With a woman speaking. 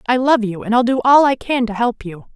Yes: female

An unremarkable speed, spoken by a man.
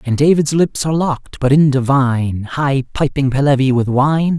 Yes: average, 180 wpm; male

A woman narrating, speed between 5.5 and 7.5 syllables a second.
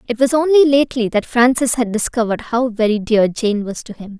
Yes: female; 5.7 syllables/s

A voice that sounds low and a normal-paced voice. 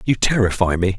Yes: low, 100 Hz; average, 180 wpm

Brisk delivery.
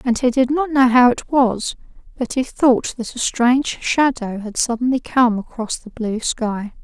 No: average, 195 wpm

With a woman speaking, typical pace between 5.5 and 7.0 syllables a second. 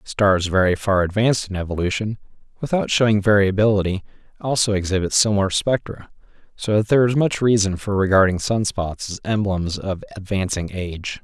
No: male; 5.6 syllables/s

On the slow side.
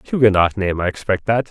No: average, 200 wpm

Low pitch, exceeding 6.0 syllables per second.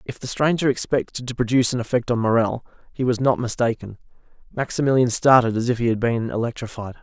Yes: low, 120 Hz; 6.2 syllables/s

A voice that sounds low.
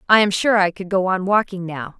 No: high, 190 Hz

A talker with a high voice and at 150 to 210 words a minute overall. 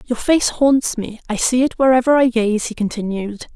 Yes: high, 235 Hz; fast, 205 wpm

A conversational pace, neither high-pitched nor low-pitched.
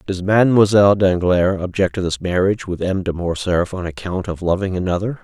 No: average, 185 wpm; very low, 95 Hz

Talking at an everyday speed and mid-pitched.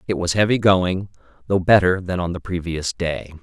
No: average, 195 wpm; very low, 90 Hz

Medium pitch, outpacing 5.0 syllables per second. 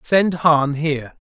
No: medium, 155 Hz; 3.7 syllables/s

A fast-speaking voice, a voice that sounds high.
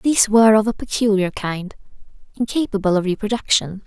No: average, 140 wpm; high, 210 Hz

